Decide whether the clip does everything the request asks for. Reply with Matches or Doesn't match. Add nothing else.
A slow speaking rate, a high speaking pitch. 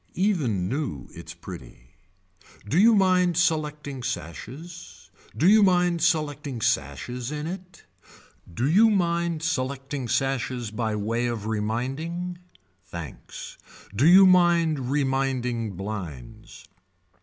Doesn't match